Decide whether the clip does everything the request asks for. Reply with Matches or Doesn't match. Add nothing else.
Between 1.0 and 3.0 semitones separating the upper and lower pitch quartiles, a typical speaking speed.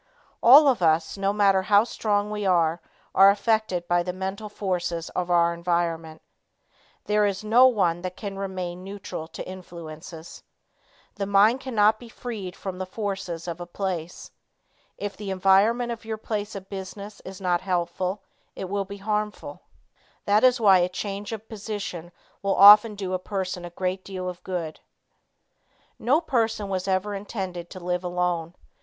Matches